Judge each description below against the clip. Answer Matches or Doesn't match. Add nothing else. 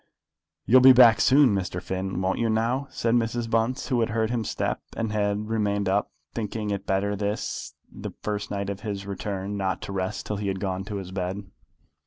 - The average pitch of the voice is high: Doesn't match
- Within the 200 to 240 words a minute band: Matches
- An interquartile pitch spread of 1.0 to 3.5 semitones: Matches